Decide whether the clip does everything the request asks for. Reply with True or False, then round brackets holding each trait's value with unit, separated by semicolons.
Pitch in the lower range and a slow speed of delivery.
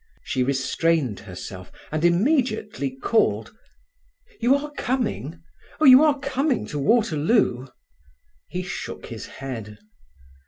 False (170 Hz; 110 wpm)